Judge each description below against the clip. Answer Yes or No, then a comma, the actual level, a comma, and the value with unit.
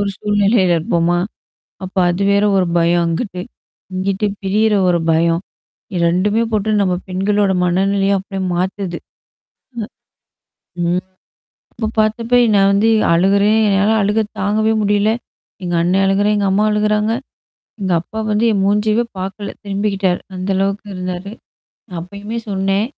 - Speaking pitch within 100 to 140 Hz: No, high, 195 Hz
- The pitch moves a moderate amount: No, narrow, 2.2 semitones